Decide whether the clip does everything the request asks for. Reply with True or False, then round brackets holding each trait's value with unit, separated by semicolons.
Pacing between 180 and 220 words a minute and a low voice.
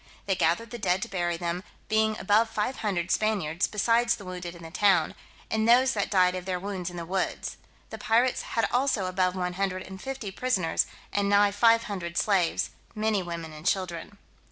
False (195 wpm; 195 Hz)